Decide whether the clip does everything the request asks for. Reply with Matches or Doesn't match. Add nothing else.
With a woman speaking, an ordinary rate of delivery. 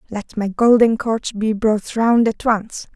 Matches